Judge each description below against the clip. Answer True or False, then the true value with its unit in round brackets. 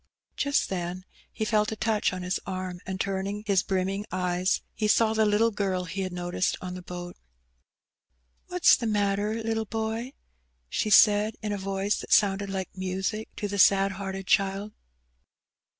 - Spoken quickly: False (175 wpm)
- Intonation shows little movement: True (2.3 semitones)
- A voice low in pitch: False (195 Hz)